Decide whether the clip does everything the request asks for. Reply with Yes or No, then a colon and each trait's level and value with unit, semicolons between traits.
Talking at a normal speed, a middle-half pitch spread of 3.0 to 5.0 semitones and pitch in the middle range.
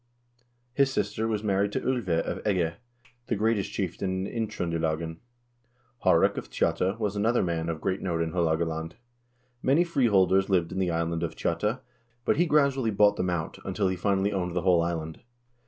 No: average, 175 wpm; average, 4.2 semitones; very low, 95 Hz